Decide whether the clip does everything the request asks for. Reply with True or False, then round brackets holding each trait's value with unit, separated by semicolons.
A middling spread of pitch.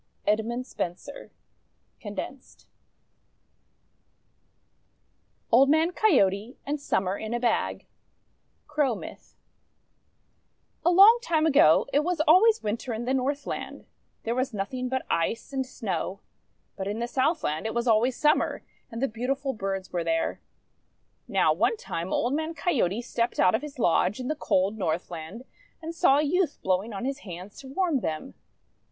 False (6.4 semitones)